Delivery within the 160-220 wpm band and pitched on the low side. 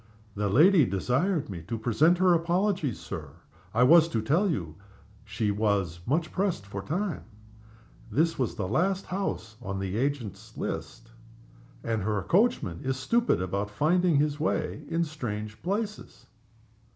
No: average, 150 wpm; low, 130 Hz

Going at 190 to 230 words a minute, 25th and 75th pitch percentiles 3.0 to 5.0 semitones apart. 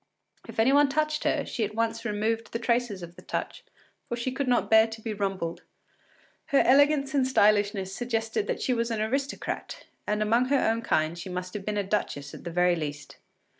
Yes: fast, 205 wpm; average, 4.0 semitones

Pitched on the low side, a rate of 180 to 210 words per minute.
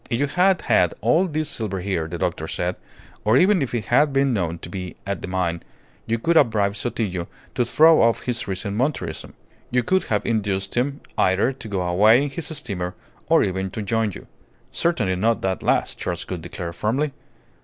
Yes: low, 110 Hz; average, 200 wpm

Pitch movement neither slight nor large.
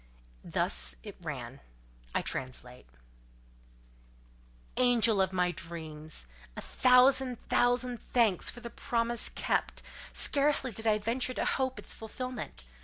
No: wide, 8.0 semitones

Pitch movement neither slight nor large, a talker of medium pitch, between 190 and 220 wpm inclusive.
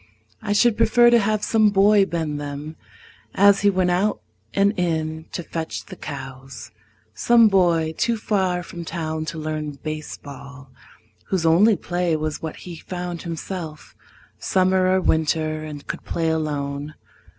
No: average, 3.7 semitones; medium, 165 Hz; average, 150 wpm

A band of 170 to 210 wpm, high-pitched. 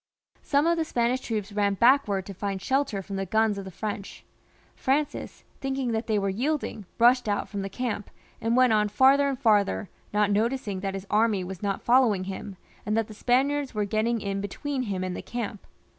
Yes: fast, 205 wpm; high, 215 Hz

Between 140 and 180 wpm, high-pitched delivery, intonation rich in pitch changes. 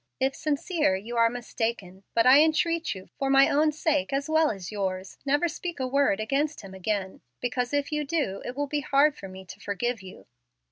No: fast, 205 wpm; very high, 265 Hz; wide, 6.6 semitones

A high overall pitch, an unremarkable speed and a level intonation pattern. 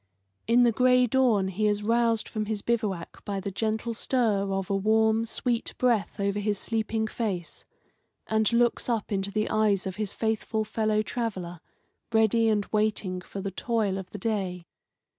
Yes: high, 215 Hz; average, 170 wpm; narrow, 2.3 semitones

